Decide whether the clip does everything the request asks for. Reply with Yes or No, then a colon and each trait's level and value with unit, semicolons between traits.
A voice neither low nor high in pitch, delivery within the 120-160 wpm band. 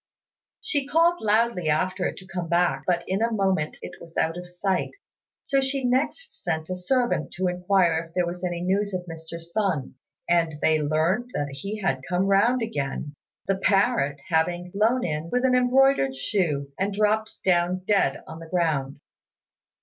No: medium, 180 Hz; average, 175 wpm